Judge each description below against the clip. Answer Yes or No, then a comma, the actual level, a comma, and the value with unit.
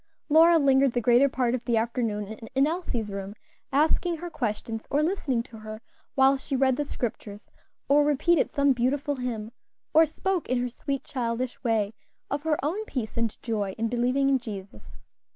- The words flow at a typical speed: Yes, average, 180 wpm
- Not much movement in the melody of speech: No, average, 4.1 semitones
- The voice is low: No, very high, 255 Hz